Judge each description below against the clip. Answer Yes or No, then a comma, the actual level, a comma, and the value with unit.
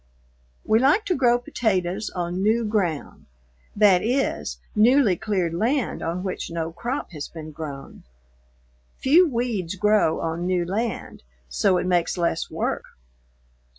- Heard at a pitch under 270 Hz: Yes, high, 190 Hz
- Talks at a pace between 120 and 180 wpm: Yes, slow, 135 wpm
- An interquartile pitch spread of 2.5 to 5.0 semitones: No, wide, 5.5 semitones